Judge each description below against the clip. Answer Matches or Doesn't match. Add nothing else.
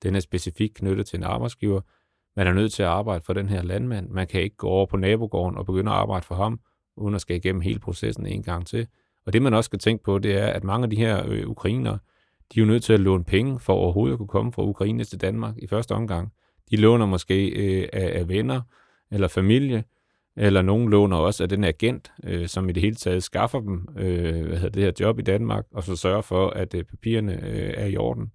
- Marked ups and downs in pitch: Doesn't match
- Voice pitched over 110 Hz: Doesn't match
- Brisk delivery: Matches